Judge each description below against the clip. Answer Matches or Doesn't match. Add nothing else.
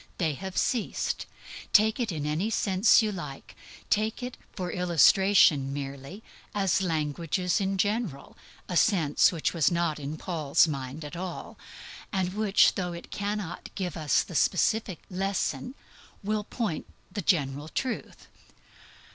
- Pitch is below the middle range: Doesn't match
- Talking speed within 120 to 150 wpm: Matches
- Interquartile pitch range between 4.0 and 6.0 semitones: Matches